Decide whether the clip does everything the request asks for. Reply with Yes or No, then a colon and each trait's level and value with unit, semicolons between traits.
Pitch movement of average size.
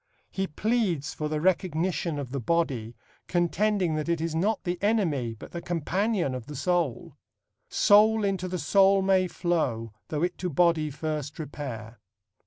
Yes: average, 4.4 semitones